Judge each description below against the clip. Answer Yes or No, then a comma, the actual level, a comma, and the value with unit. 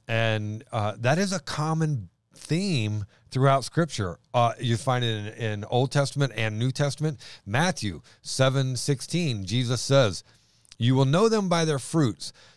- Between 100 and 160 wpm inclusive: Yes, average, 150 wpm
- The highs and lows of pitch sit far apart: No, average, 4.6 semitones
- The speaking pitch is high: No, low, 130 Hz